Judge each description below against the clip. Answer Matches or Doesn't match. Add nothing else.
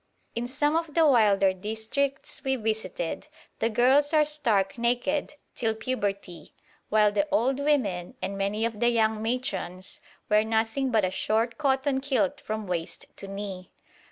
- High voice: Matches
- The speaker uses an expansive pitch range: Doesn't match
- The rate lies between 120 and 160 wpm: Matches